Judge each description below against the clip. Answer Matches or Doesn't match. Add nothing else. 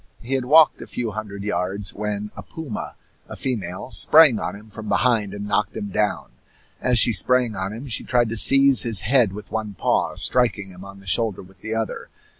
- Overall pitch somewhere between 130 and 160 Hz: Doesn't match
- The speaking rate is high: Matches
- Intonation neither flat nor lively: Matches